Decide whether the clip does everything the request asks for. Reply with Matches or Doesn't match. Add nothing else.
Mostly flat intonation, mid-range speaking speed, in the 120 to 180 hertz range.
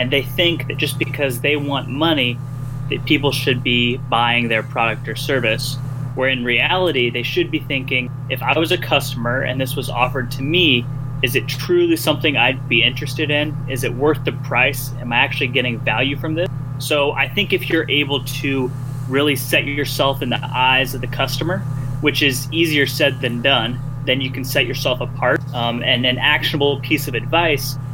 Matches